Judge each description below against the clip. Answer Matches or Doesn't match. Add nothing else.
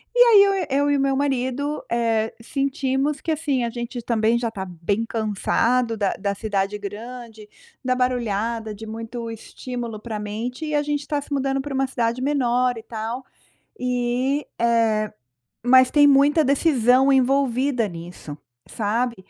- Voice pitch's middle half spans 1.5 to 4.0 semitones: Matches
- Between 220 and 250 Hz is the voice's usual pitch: Matches